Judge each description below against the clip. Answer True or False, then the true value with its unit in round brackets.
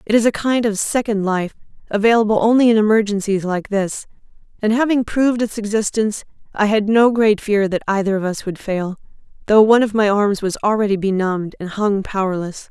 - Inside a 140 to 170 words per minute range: False (190 wpm)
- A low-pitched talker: False (210 Hz)